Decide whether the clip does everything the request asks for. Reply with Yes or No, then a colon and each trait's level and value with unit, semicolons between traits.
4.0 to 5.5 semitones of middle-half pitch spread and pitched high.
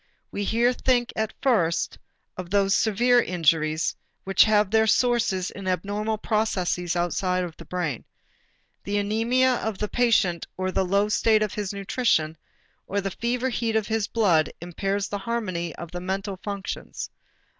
No: average, 3.4 semitones; high, 200 Hz